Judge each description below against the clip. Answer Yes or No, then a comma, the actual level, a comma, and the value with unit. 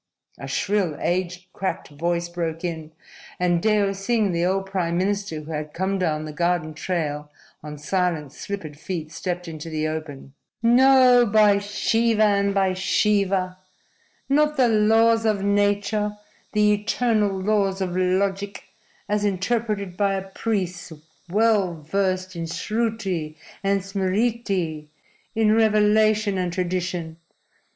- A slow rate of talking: Yes, slow, 130 wpm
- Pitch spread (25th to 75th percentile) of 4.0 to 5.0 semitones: No, average, 3.4 semitones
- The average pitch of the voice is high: Yes, high, 195 Hz